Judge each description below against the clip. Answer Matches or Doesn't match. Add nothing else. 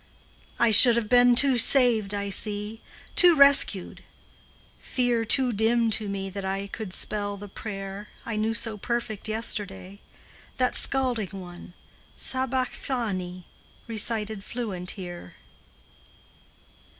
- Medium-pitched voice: Doesn't match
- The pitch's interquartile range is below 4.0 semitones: Matches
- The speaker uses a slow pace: Matches